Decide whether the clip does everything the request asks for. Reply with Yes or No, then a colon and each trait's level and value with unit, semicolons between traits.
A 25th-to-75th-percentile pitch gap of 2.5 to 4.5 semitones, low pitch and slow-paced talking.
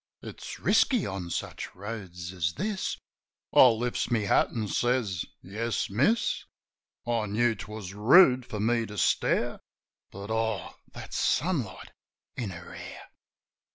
Yes: average, 3.5 semitones; low, 110 Hz; slow, 130 wpm